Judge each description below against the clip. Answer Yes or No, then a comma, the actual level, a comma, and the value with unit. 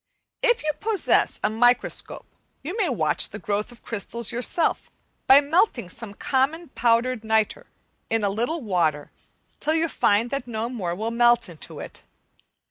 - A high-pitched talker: Yes, high, 235 Hz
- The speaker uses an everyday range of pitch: Yes, average, 5.0 semitones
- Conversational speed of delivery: Yes, average, 155 wpm